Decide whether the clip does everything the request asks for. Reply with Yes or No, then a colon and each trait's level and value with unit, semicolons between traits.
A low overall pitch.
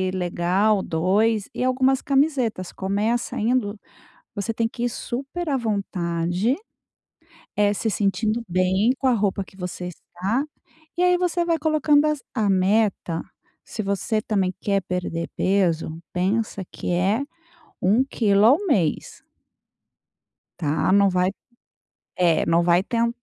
No: high, 205 Hz